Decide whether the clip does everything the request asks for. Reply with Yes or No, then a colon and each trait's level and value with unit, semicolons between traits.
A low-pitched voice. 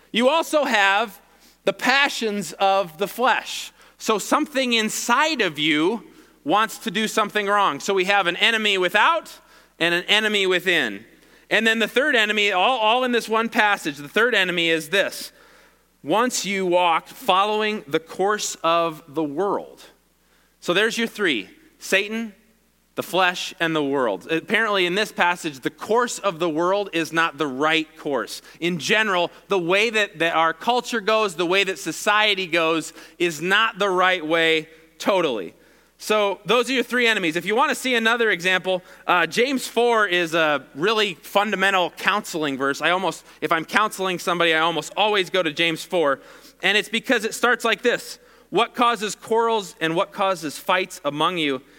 No: high, 195 Hz